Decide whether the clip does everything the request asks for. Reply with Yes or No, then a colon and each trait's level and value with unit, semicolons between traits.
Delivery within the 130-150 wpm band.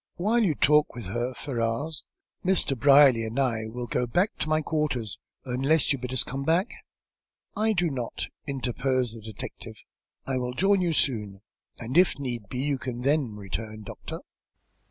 No: average, 170 wpm